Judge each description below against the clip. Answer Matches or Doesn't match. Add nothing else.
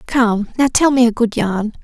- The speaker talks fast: Matches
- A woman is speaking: Matches